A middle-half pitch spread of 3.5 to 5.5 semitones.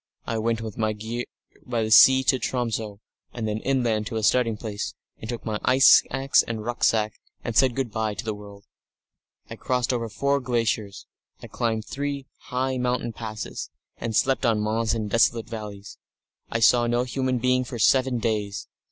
No: narrow, 2.5 semitones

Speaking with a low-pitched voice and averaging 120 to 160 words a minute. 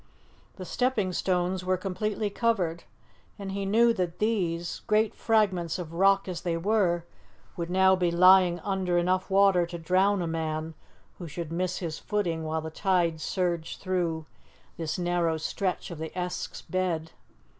No: medium, 180 Hz; average, 155 wpm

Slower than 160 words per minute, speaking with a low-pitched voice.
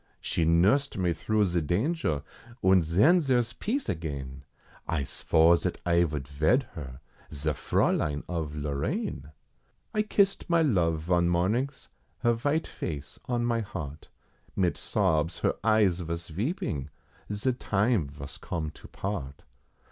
Yes: average, 140 wpm; very low, 85 Hz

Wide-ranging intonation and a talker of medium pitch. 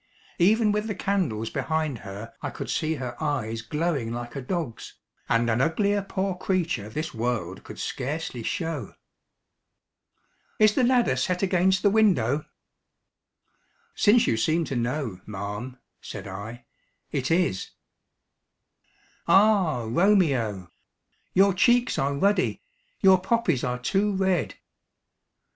Yes: wide, 8.3 semitones; medium, 155 Hz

